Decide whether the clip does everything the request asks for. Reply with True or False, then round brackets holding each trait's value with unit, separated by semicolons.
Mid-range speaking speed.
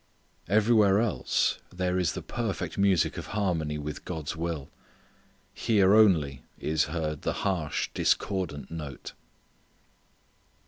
False (110 wpm)